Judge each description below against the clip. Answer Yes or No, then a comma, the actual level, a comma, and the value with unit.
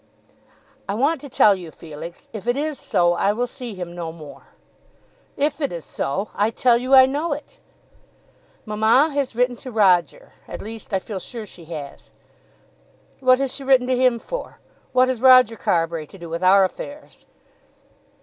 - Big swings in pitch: Yes, wide, 6.2 semitones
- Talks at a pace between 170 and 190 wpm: Yes, average, 180 wpm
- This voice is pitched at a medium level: No, high, 230 Hz